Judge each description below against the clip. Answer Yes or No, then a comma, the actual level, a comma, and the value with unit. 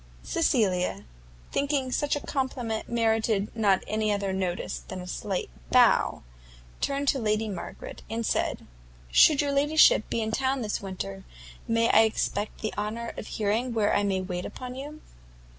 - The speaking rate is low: No, average, 160 wpm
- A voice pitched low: No, high, 220 Hz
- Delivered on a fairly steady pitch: No, average, 4.4 semitones